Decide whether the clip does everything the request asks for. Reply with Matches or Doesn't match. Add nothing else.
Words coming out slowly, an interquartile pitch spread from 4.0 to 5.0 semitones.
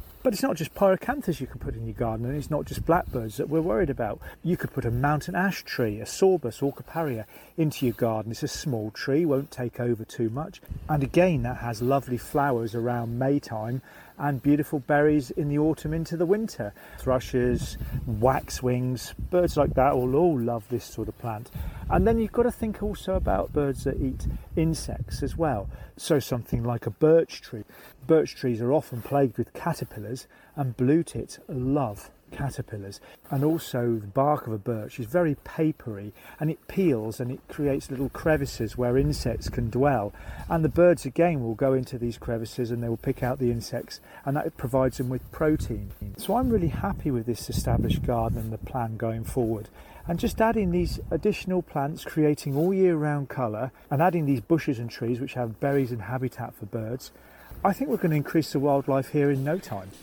Doesn't match